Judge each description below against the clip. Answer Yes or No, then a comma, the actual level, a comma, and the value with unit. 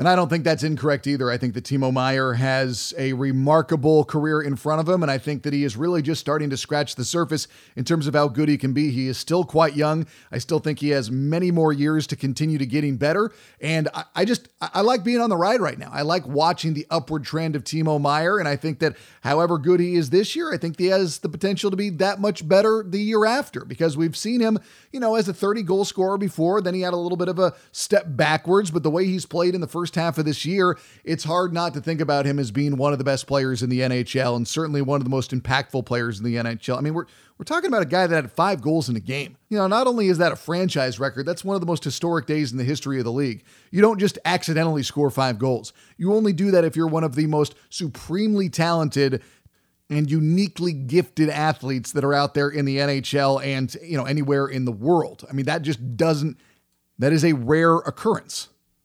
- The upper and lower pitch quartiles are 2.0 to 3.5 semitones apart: No, average, 4.1 semitones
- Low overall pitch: No, medium, 155 Hz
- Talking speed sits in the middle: No, fast, 255 wpm